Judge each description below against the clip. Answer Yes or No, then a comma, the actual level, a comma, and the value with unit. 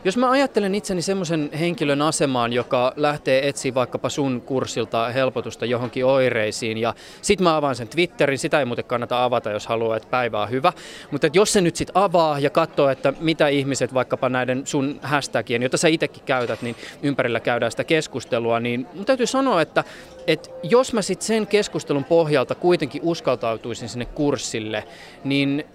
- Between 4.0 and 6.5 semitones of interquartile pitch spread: Yes, average, 5.2 semitones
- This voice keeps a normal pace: No, fast, 175 wpm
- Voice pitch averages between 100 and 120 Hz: No, medium, 140 Hz